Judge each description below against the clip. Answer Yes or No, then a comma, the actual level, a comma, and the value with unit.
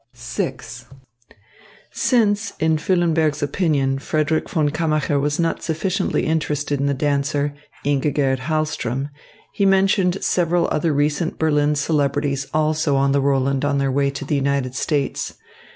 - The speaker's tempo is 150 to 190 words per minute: No, slow, 135 wpm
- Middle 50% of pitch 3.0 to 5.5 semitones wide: No, narrow, 2.4 semitones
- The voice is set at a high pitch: No, medium, 150 Hz